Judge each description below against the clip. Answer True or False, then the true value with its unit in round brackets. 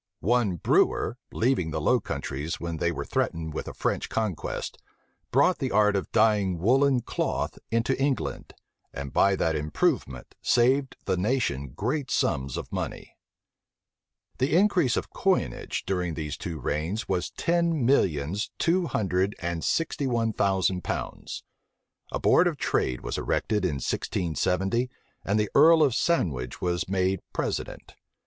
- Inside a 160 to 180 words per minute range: False (145 wpm)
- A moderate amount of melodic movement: False (7.5 semitones)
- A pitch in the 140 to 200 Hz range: False (100 Hz)